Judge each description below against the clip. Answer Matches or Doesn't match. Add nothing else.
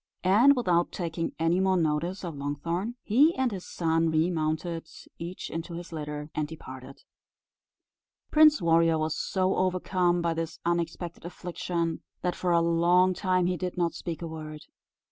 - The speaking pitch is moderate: Matches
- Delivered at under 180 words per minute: Matches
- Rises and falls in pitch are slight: Matches